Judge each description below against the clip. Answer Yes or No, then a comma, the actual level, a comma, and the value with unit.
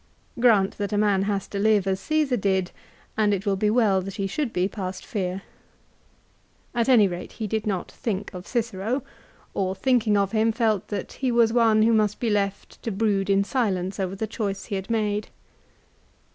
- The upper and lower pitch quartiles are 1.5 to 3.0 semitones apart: Yes, narrow, 2.6 semitones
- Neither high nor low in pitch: No, high, 205 Hz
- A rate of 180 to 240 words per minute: Yes, average, 195 wpm